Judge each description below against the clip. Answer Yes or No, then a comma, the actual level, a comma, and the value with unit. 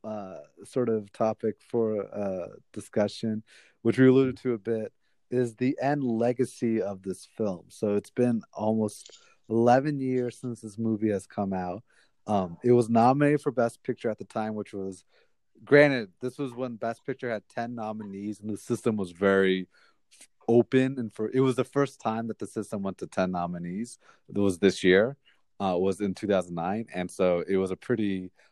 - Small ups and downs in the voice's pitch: No, average, 3.7 semitones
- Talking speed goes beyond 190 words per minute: No, average, 185 wpm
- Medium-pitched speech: No, low, 110 Hz